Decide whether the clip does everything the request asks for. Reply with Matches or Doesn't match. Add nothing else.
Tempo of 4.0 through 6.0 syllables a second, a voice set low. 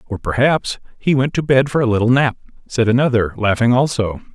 Matches